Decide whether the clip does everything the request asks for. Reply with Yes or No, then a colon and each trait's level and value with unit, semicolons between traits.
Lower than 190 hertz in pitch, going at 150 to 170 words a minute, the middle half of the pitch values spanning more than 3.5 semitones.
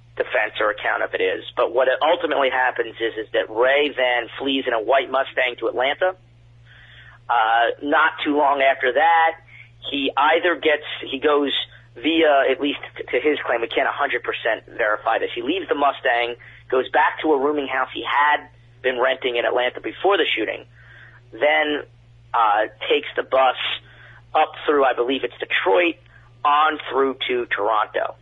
Yes: medium, 140 Hz; average, 165 wpm; wide, 5.4 semitones